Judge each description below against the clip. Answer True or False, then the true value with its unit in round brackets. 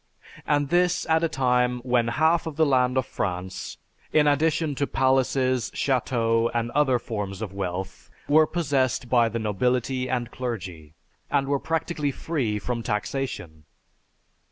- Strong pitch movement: False (4.0 semitones)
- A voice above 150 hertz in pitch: False (125 Hz)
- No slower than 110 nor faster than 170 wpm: True (140 wpm)